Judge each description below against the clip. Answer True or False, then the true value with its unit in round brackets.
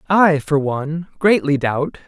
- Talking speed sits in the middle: True (145 wpm)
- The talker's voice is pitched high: False (155 Hz)